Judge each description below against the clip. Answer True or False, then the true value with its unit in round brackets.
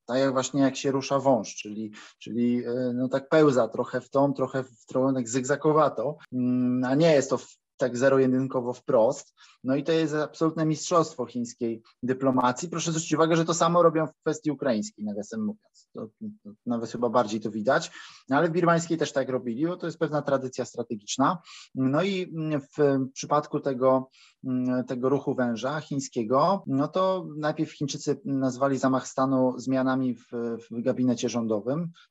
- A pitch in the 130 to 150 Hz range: True (135 Hz)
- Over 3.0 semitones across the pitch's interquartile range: True (3.7 semitones)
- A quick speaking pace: True (170 wpm)